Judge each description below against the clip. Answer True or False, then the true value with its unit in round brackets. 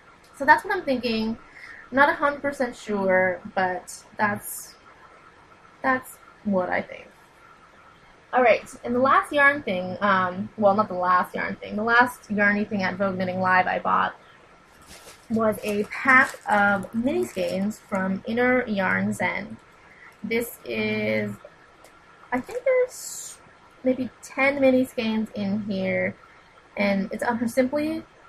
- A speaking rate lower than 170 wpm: True (140 wpm)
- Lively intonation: True (5.7 semitones)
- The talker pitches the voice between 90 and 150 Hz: False (220 Hz)